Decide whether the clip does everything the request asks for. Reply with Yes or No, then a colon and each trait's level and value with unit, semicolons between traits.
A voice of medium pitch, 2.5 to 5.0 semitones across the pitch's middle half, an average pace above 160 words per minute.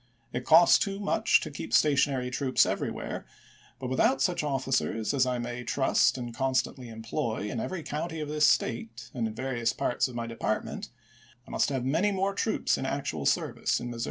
No: low, 130 Hz; average, 3.9 semitones; average, 190 wpm